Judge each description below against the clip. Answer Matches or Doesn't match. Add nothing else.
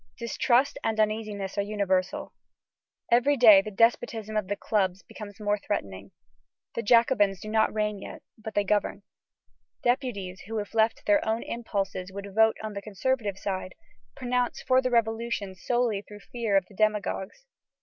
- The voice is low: Doesn't match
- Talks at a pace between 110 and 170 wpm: Matches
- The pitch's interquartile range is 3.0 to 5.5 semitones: Doesn't match